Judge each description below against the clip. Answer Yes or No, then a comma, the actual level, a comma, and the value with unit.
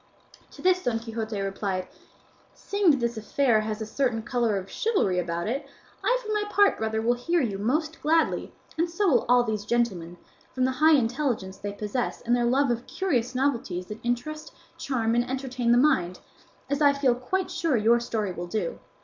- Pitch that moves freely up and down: No, average, 4.7 semitones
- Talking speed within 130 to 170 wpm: No, average, 190 wpm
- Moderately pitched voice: No, high, 240 Hz